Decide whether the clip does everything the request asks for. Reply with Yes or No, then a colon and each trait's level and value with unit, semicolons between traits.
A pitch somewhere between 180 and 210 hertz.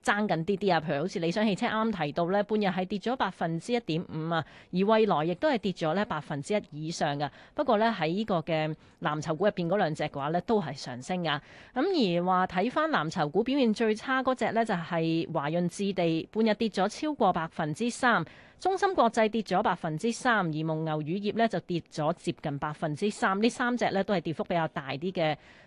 Yes: medium, 185 Hz